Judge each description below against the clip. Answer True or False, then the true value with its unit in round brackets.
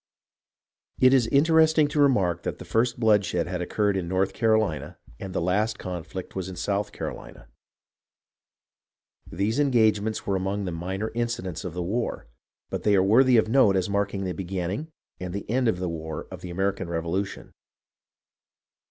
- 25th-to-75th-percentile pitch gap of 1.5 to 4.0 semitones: True (3.7 semitones)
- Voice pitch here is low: True (100 Hz)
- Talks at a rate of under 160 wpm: False (165 wpm)